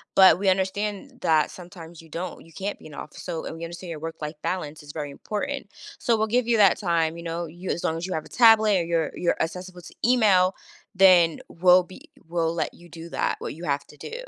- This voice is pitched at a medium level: Yes, medium, 175 Hz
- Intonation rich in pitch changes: No, average, 2.8 semitones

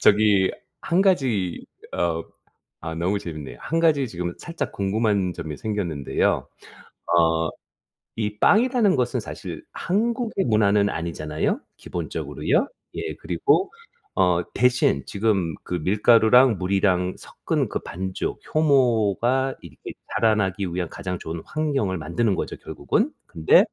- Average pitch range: No, wide, 6.5 semitones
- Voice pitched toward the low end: Yes, low, 100 Hz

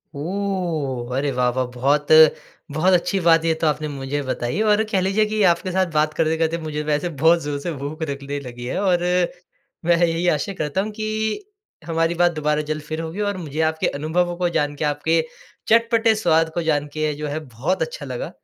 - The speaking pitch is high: No, medium, 160 Hz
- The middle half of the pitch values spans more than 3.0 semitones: Yes, average, 3.8 semitones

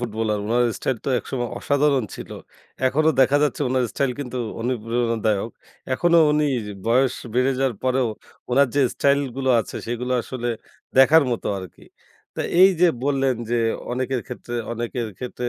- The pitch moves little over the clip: Yes, narrow, 2.3 semitones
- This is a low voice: Yes, low, 125 Hz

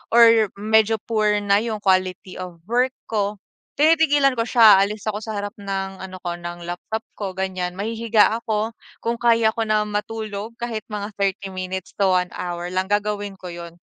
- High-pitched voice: Yes, high, 205 Hz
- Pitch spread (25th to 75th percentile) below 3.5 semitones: Yes, average, 2.9 semitones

